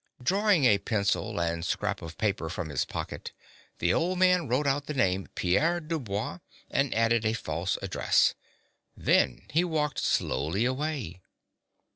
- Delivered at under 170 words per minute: Yes, average, 150 wpm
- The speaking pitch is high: No, low, 115 Hz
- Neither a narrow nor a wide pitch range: No, wide, 8.7 semitones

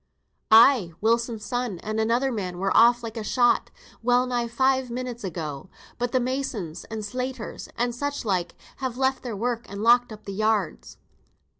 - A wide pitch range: No, average, 2.9 semitones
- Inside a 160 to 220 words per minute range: Yes, average, 170 wpm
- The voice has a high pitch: Yes, high, 235 Hz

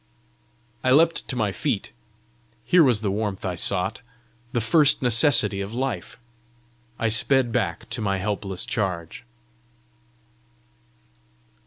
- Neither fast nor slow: No, slow, 120 wpm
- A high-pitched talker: No, low, 110 Hz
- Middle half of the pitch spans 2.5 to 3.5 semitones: No, average, 4.6 semitones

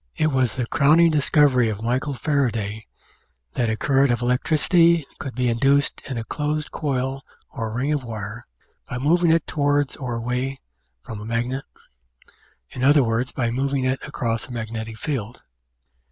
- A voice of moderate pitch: No, low, 130 Hz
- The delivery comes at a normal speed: Yes, average, 160 wpm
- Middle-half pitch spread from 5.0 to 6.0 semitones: No, average, 3.6 semitones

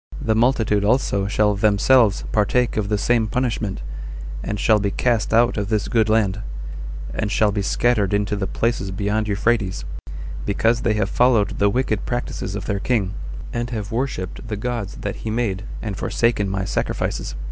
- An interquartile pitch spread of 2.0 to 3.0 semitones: Yes, narrow, 2.6 semitones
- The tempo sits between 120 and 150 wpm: No, average, 170 wpm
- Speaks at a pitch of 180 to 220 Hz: No, low, 105 Hz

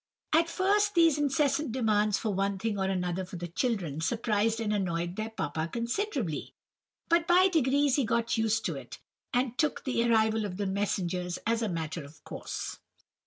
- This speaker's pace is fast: No, average, 175 wpm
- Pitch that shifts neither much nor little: No, wide, 6.0 semitones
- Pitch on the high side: Yes, high, 220 Hz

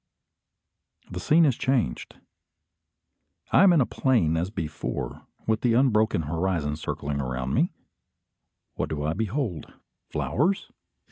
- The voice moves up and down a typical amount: No, wide, 8.8 semitones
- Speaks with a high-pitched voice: No, very low, 95 Hz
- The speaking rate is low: Yes, slow, 125 wpm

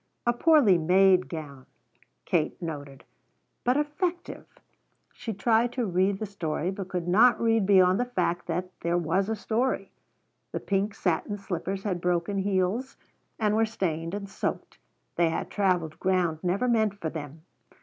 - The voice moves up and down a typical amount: Yes, average, 4.0 semitones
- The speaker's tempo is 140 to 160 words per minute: Yes, average, 155 wpm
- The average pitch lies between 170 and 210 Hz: Yes, high, 190 Hz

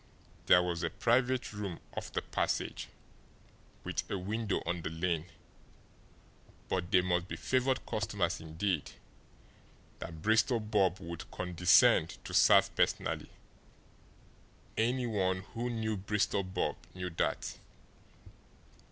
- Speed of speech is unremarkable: No, slow, 115 wpm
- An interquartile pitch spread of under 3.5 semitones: No, average, 3.9 semitones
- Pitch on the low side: Yes, very low, 95 Hz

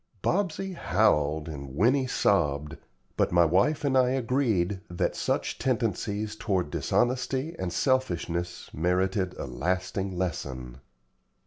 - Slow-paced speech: Yes, slow, 115 wpm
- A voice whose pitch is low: Yes, very low, 95 Hz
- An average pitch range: No, wide, 6.9 semitones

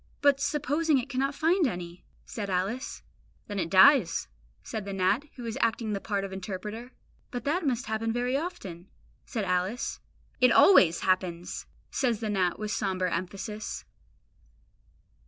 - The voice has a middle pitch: No, high, 215 Hz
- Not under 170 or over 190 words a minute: No, average, 150 wpm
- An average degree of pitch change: No, wide, 5.7 semitones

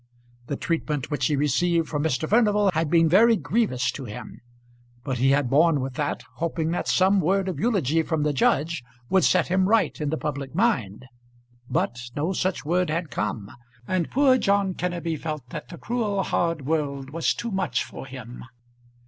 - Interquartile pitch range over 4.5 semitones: Yes, average, 4.9 semitones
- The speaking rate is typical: Yes, average, 180 wpm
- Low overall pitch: No, medium, 160 Hz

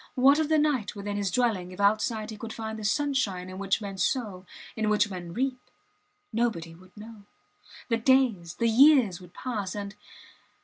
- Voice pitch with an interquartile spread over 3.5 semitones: Yes, average, 4.3 semitones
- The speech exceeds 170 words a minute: Yes, average, 180 wpm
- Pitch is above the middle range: Yes, high, 215 Hz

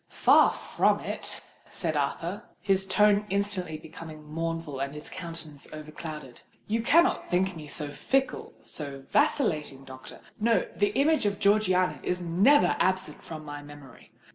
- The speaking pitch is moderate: Yes, medium, 170 Hz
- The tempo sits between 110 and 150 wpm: Yes, average, 140 wpm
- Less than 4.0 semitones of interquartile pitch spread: No, average, 5.2 semitones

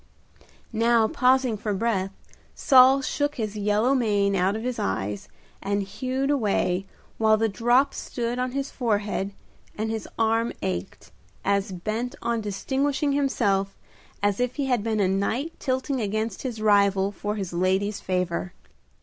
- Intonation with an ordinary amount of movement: Yes, average, 4.0 semitones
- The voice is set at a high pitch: Yes, high, 220 Hz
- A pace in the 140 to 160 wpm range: Yes, average, 150 wpm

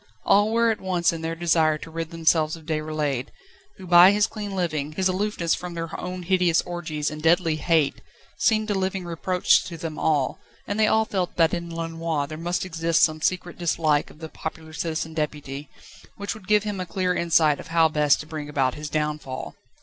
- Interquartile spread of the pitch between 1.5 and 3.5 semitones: Yes, average, 2.8 semitones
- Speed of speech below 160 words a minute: No, fast, 205 wpm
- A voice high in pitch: No, medium, 165 Hz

